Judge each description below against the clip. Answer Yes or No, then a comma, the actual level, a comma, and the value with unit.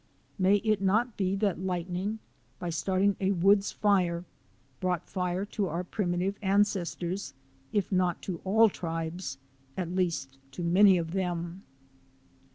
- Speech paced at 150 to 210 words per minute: No, average, 140 wpm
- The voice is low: No, medium, 185 Hz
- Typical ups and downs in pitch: No, narrow, 2.3 semitones